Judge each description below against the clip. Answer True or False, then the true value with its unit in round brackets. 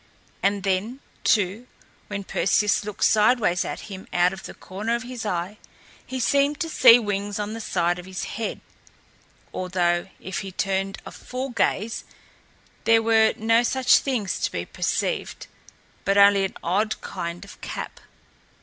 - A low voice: False (205 Hz)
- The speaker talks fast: False (160 wpm)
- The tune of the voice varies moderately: True (3.3 semitones)